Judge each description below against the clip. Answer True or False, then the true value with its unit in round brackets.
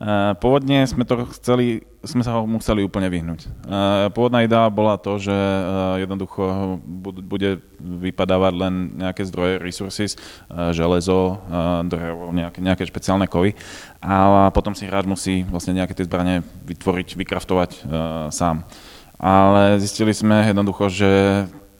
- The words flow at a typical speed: True (125 wpm)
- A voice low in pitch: True (95 Hz)